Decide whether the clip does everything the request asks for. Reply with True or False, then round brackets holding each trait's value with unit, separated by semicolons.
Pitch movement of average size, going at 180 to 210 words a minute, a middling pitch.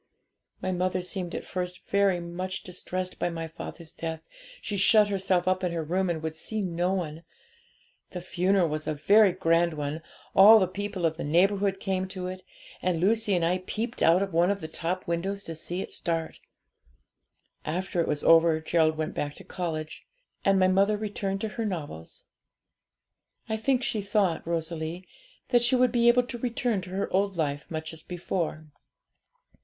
True (3.2 semitones; 185 wpm; 180 Hz)